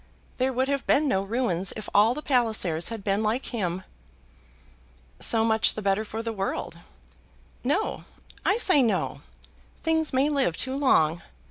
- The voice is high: Yes, high, 230 Hz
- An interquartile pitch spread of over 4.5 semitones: Yes, average, 5.2 semitones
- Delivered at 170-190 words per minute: No, average, 155 wpm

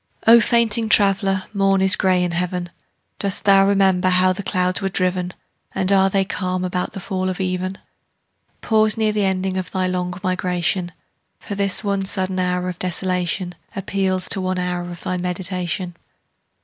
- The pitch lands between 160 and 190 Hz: Yes, medium, 185 Hz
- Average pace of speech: Yes, average, 170 wpm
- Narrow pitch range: Yes, narrow, 1.3 semitones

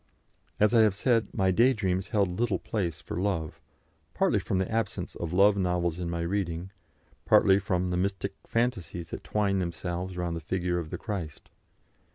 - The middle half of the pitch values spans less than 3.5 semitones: Yes, average, 2.7 semitones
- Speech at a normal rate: Yes, average, 180 wpm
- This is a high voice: No, very low, 95 Hz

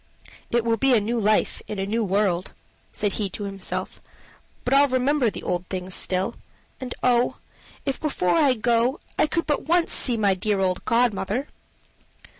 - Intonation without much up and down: No, average, 4.7 semitones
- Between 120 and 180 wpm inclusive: Yes, average, 175 wpm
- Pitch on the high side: Yes, high, 230 Hz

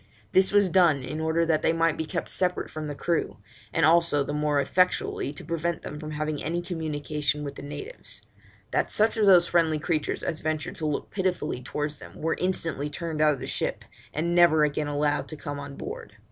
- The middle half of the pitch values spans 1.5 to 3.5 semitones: Yes, narrow, 2.5 semitones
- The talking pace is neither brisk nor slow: No, fast, 210 wpm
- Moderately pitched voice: Yes, medium, 155 Hz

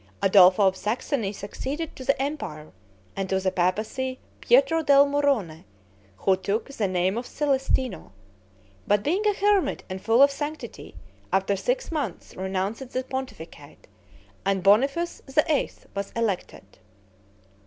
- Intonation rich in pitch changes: Yes, wide, 6.7 semitones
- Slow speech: Yes, slow, 130 wpm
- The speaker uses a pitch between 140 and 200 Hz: No, high, 235 Hz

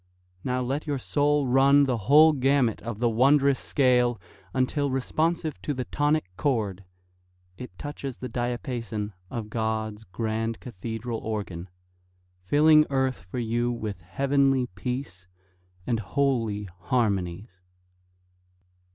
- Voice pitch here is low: Yes, low, 125 Hz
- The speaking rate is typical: No, slow, 115 wpm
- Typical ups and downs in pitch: Yes, average, 4.1 semitones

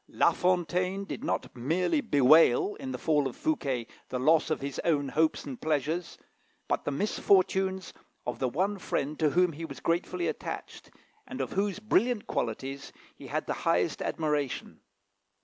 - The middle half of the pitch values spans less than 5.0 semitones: No, average, 5.3 semitones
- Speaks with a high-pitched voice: No, medium, 165 Hz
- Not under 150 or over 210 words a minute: Yes, average, 165 wpm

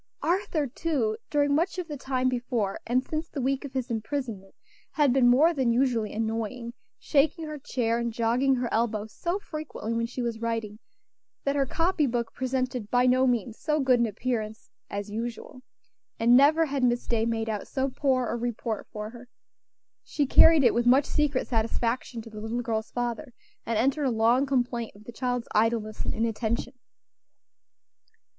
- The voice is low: No, high, 245 Hz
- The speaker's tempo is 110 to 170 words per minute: No, average, 180 wpm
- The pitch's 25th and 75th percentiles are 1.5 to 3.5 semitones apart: Yes, average, 3.2 semitones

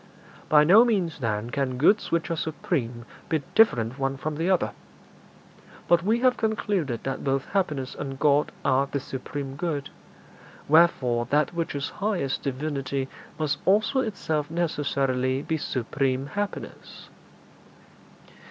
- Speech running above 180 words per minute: No, slow, 135 wpm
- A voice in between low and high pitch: Yes, medium, 145 Hz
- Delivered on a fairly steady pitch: No, average, 4.3 semitones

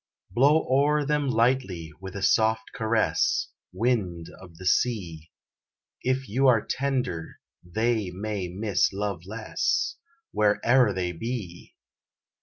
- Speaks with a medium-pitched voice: No, low, 110 Hz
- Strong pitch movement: Yes, wide, 5.7 semitones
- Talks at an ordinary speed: No, slow, 120 wpm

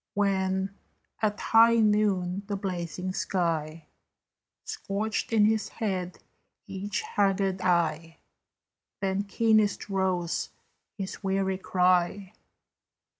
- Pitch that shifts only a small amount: Yes, narrow, 2.1 semitones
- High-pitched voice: Yes, high, 195 Hz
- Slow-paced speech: Yes, slow, 90 wpm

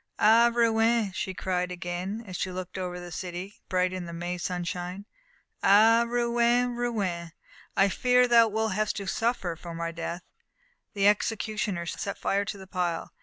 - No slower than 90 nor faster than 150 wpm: No, average, 165 wpm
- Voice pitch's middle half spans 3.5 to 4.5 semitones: Yes, average, 4.0 semitones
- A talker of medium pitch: No, high, 195 Hz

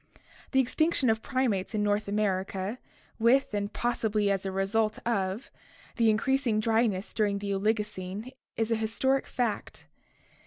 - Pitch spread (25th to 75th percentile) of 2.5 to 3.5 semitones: Yes, average, 2.8 semitones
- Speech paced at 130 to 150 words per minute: Yes, average, 145 wpm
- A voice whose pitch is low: No, high, 215 Hz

